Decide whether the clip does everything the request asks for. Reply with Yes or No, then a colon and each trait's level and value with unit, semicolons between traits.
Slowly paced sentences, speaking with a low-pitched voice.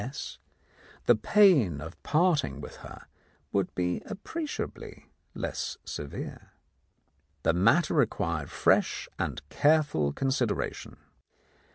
Yes: slow, 100 wpm; low, 115 Hz